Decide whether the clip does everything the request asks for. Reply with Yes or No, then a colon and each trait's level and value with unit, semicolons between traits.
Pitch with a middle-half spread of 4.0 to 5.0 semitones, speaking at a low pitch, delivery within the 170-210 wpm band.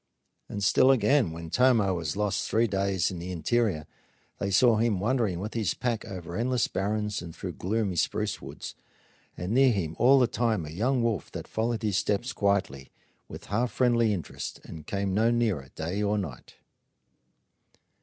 Yes: average, 4.4 semitones; low, 105 Hz; average, 175 wpm